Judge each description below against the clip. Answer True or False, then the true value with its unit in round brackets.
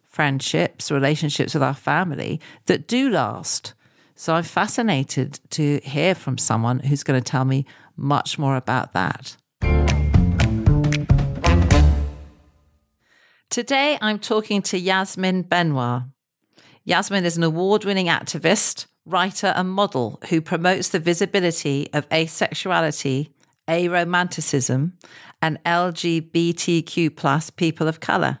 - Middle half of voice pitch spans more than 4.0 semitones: True (4.9 semitones)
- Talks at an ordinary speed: False (110 wpm)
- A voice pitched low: False (160 Hz)